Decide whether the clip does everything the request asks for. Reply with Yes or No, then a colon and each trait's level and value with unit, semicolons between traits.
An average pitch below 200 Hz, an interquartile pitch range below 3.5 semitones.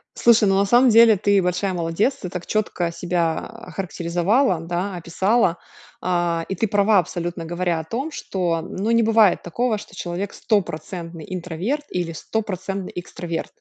No: medium, 185 Hz; average, 3.8 semitones